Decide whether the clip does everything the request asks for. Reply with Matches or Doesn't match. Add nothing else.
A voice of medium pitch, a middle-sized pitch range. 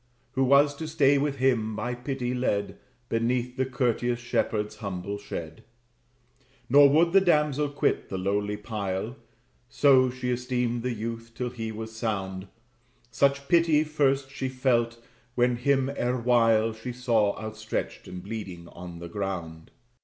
Doesn't match